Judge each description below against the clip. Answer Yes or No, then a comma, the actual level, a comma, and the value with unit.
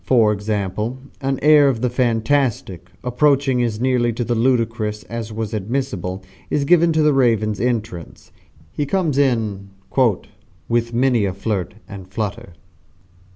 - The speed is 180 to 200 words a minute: No, average, 140 wpm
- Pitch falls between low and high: No, low, 115 Hz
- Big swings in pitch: No, average, 3.9 semitones